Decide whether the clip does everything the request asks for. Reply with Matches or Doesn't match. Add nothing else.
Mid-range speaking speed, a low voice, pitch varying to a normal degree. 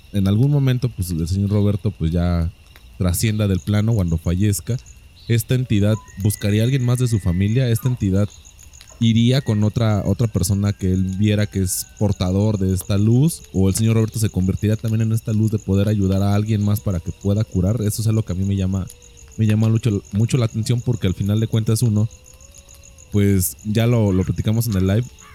Doesn't match